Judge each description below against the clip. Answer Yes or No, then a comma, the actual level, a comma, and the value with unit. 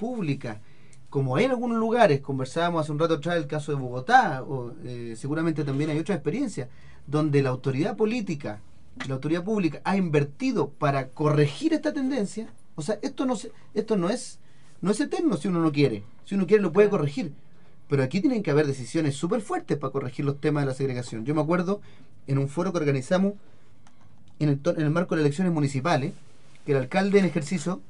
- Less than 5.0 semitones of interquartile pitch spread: No, wide, 5.5 semitones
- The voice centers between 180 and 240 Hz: No, medium, 150 Hz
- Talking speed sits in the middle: No, fast, 200 wpm